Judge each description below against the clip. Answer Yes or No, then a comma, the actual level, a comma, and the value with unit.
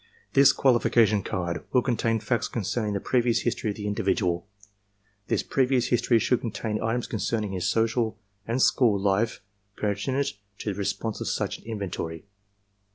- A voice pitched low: Yes, low, 110 Hz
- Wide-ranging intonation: No, average, 2.9 semitones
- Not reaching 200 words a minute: Yes, average, 160 wpm